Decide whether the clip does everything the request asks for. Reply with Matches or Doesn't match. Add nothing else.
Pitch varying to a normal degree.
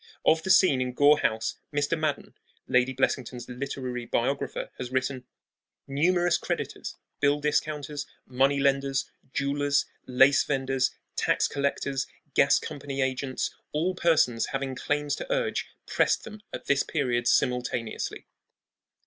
Doesn't match